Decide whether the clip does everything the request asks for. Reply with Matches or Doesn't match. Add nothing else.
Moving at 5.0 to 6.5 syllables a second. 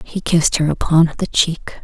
Doesn't match